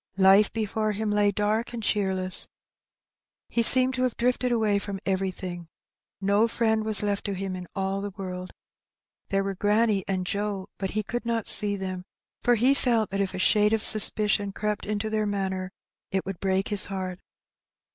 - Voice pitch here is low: No, high, 205 Hz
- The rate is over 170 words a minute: Yes, average, 185 wpm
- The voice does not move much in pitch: Yes, narrow, 2.2 semitones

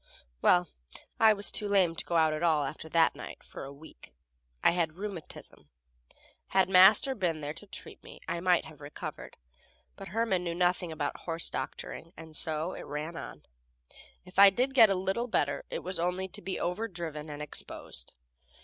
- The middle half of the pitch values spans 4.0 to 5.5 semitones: No, average, 3.3 semitones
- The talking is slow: No, average, 185 wpm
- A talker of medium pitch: Yes, medium, 175 Hz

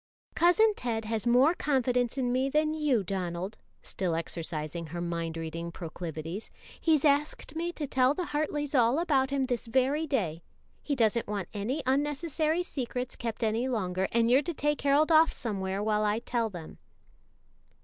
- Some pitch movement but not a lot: No, wide, 7.2 semitones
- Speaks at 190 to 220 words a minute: No, average, 165 wpm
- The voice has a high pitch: Yes, high, 245 Hz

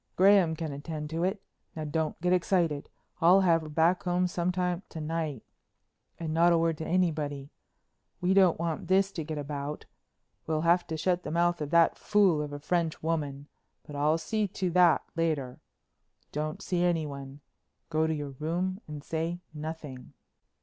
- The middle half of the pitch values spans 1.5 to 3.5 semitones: Yes, average, 2.8 semitones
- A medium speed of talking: Yes, average, 170 wpm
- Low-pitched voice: No, medium, 165 Hz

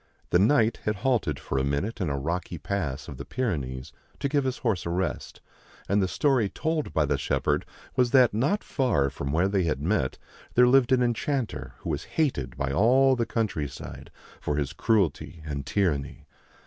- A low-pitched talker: Yes, very low, 95 Hz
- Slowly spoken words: No, average, 185 wpm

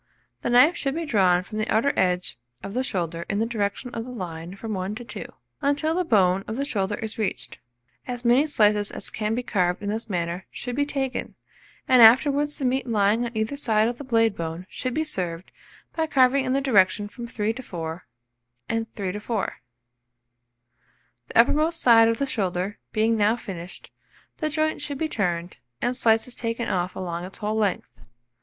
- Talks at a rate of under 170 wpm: No, average, 195 wpm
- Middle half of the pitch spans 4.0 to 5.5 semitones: Yes, average, 4.8 semitones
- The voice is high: Yes, high, 225 Hz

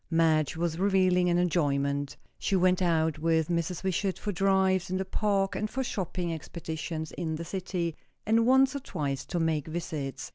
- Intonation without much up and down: No, average, 3.1 semitones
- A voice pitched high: No, medium, 175 Hz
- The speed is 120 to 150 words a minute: No, average, 175 wpm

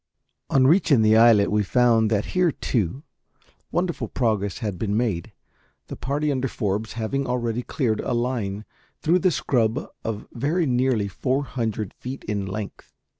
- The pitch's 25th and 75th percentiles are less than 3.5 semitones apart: No, average, 4.0 semitones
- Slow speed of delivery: No, average, 155 wpm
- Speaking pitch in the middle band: No, low, 115 Hz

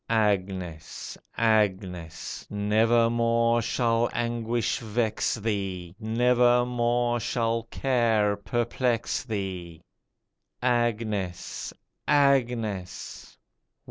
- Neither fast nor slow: No, slow, 60 wpm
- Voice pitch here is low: Yes, low, 115 Hz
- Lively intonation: No, average, 2.7 semitones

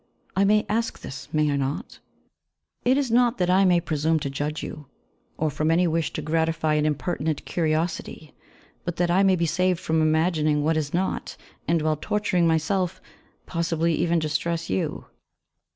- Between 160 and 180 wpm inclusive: Yes, average, 170 wpm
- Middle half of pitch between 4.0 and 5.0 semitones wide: No, average, 2.8 semitones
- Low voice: No, medium, 165 Hz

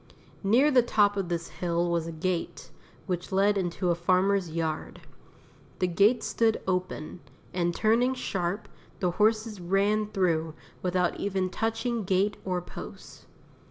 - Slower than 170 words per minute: Yes, average, 140 wpm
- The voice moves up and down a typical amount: Yes, average, 3.3 semitones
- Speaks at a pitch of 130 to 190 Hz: Yes, medium, 185 Hz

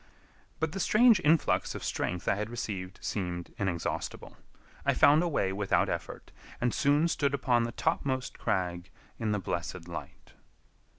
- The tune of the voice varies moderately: No, wide, 7.8 semitones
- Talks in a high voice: No, low, 115 Hz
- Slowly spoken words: No, average, 155 wpm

